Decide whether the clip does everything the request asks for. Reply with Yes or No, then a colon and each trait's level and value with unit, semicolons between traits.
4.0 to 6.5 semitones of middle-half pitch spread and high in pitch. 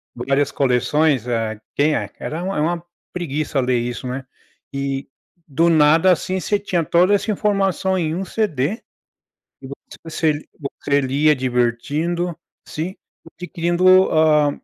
No: average, 4.4 semitones; medium, 155 Hz